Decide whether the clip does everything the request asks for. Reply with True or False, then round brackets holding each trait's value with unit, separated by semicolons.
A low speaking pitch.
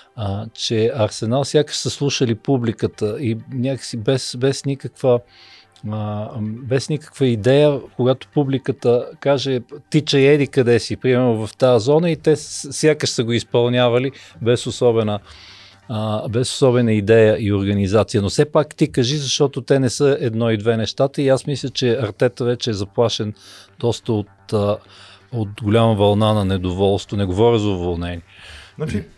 True (120 Hz)